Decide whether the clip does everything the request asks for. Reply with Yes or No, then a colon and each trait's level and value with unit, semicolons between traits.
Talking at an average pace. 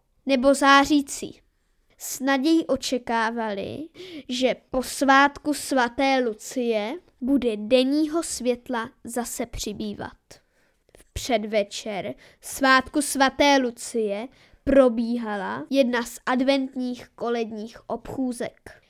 No: slow, 80 wpm